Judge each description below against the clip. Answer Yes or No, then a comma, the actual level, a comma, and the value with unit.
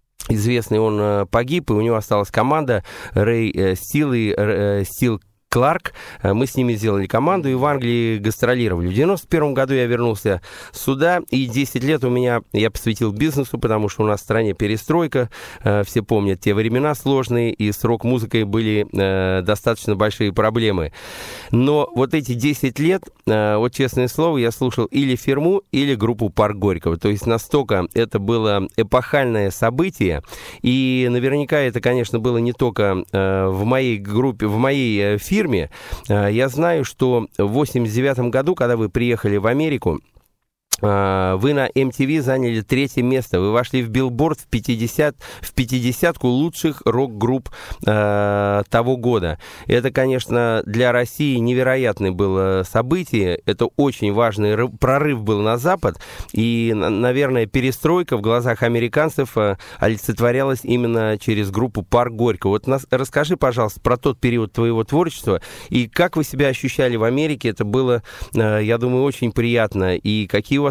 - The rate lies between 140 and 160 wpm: Yes, average, 150 wpm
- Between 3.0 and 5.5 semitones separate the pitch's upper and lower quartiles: Yes, average, 3.8 semitones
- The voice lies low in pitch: Yes, low, 120 Hz